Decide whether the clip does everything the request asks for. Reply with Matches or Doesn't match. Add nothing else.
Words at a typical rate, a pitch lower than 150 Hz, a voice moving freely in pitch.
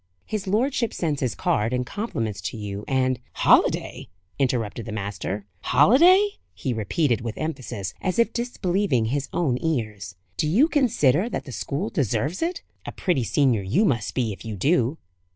Matches